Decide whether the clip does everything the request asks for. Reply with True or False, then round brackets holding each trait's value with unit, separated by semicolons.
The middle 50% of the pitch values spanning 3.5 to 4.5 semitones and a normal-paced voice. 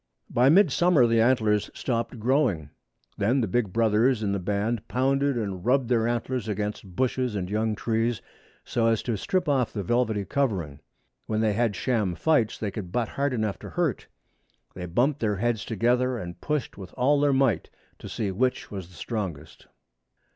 True (3.9 semitones; 180 wpm)